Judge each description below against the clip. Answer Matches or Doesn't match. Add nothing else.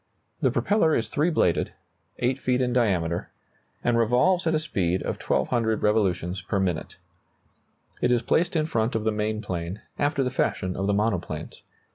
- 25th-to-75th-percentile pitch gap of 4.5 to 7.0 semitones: Matches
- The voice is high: Doesn't match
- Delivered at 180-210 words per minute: Doesn't match